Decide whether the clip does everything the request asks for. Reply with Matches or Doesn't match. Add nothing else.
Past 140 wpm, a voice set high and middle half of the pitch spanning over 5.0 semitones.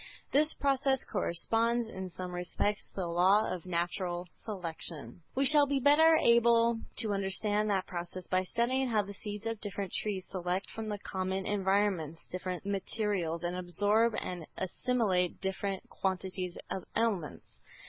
Doesn't match